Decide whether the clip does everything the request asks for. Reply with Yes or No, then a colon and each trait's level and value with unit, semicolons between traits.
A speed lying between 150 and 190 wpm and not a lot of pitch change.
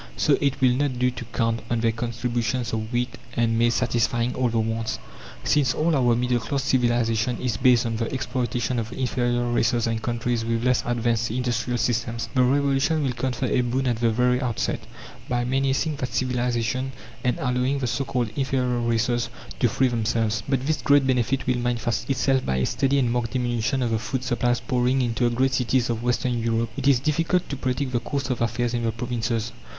No: average, 200 wpm; narrow, 1.8 semitones